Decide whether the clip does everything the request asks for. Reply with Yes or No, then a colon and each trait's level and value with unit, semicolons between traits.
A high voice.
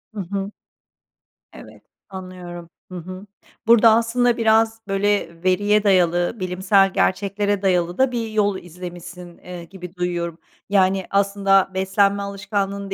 Yes: high, 195 Hz